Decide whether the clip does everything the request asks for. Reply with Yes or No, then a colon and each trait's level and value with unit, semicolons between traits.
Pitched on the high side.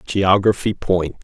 No: very low, 95 Hz